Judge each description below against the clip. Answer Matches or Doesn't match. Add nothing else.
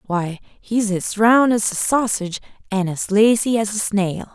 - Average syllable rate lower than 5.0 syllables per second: Matches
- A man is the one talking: Doesn't match